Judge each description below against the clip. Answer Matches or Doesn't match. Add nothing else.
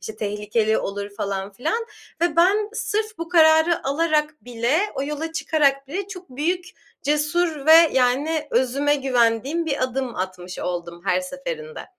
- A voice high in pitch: Matches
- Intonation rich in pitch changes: Matches